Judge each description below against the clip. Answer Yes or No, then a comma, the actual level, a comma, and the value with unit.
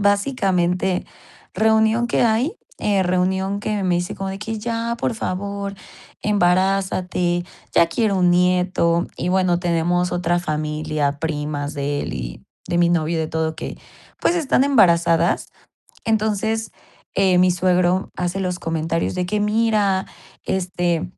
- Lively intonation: No, average, 2.9 semitones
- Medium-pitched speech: Yes, medium, 180 Hz